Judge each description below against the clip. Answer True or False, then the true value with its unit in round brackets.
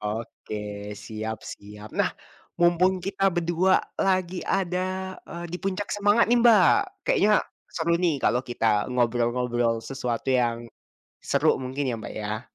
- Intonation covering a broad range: True (8.4 semitones)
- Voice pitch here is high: False (135 Hz)